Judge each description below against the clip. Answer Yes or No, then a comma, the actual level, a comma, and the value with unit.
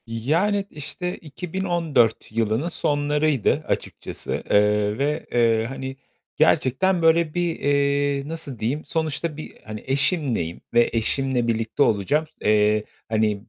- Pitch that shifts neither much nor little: No, wide, 5.9 semitones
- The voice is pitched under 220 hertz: Yes, medium, 140 Hz